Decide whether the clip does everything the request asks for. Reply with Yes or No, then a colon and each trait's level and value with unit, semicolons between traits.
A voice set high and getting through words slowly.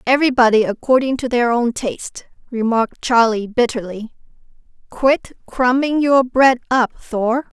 Yes: high, 245 Hz; slow, 120 wpm